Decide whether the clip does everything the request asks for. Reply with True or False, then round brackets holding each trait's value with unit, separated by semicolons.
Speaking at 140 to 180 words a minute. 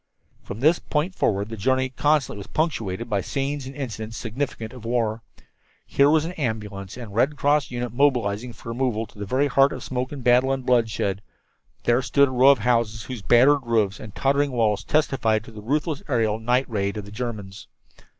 False (195 wpm)